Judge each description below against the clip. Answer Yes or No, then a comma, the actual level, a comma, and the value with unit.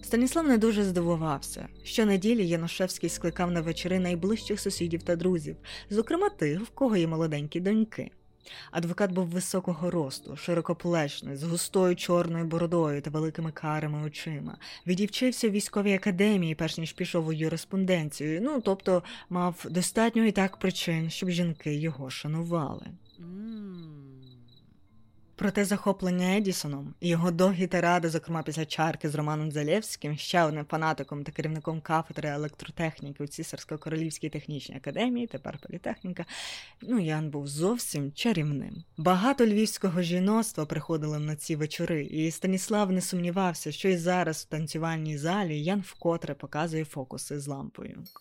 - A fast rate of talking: No, average, 135 wpm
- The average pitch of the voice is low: No, medium, 170 Hz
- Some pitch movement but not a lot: Yes, average, 3.6 semitones